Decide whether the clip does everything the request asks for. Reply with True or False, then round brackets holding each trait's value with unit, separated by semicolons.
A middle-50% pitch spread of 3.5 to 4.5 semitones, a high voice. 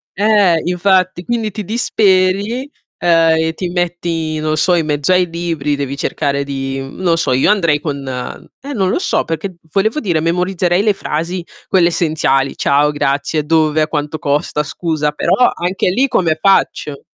False (4.0 semitones; 170 Hz)